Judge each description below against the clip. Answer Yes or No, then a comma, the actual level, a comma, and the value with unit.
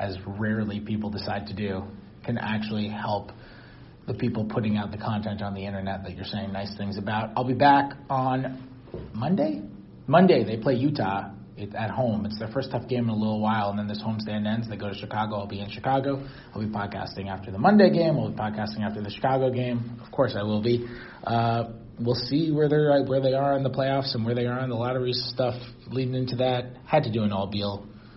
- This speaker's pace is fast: Yes, fast, 220 wpm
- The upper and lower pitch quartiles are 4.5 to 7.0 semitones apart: No, average, 3.6 semitones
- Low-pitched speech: Yes, low, 110 Hz